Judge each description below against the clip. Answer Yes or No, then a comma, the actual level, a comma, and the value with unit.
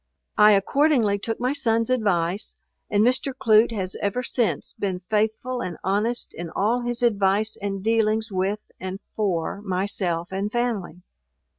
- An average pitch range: Yes, average, 3.3 semitones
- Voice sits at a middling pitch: No, high, 210 Hz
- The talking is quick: No, average, 145 wpm